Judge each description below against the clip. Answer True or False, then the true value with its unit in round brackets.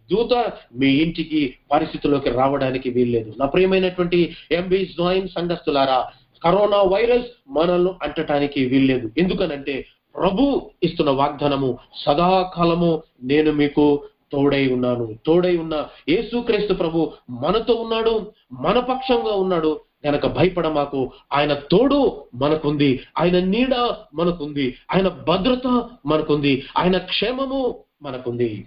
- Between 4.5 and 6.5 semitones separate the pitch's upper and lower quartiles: True (5.0 semitones)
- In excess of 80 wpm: True (105 wpm)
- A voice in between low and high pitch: True (160 Hz)